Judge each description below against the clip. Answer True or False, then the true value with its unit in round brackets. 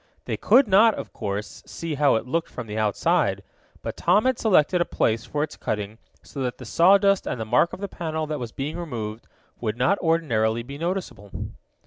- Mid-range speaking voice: True (145 Hz)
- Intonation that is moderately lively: False (7.6 semitones)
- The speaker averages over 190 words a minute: True (200 wpm)